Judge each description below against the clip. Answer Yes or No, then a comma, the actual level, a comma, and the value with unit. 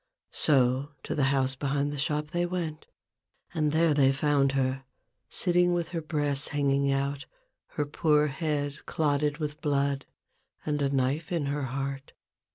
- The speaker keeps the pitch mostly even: Yes, narrow, 1.9 semitones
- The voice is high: No, medium, 145 Hz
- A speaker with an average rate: Yes, average, 160 wpm